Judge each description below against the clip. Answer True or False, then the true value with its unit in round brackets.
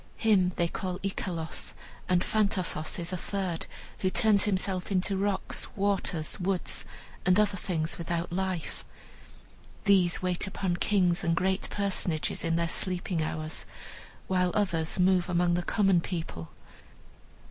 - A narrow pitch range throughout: True (2.3 semitones)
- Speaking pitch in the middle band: True (180 Hz)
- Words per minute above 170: False (135 wpm)